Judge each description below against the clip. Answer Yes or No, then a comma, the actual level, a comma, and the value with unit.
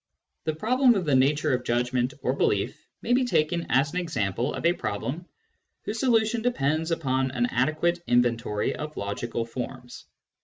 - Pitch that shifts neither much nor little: No, wide, 6.0 semitones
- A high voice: No, medium, 145 Hz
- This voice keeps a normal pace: Yes, average, 160 wpm